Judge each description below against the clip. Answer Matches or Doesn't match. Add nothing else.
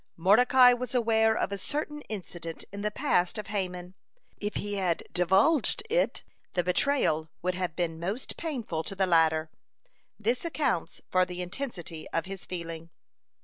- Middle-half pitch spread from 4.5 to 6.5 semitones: Matches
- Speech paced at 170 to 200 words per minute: Doesn't match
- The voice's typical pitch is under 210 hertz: Matches